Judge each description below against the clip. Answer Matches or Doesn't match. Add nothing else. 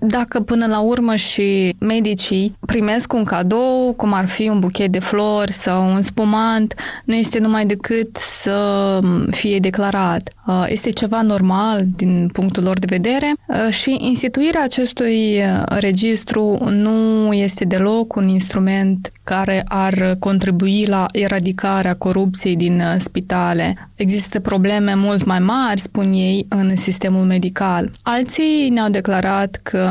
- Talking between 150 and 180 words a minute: Doesn't match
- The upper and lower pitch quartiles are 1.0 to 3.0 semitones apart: Matches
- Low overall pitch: Doesn't match